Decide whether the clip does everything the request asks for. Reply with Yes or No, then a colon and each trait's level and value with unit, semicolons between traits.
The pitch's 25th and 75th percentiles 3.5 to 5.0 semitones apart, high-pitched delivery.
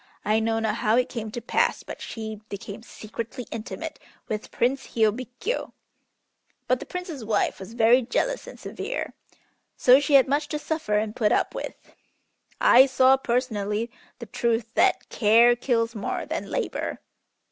No: average, 3.0 semitones; high, 235 Hz